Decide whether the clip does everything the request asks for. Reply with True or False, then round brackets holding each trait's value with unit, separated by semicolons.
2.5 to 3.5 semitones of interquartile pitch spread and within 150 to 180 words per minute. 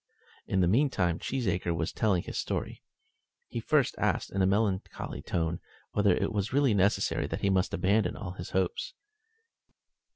True (2.8 semitones; 160 wpm)